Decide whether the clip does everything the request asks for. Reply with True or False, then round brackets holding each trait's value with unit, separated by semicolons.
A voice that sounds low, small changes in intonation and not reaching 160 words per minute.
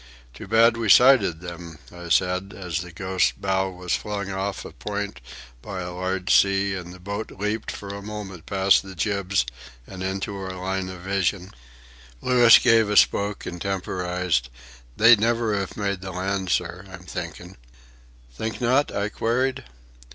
False (95 Hz; 2.1 semitones; 165 wpm)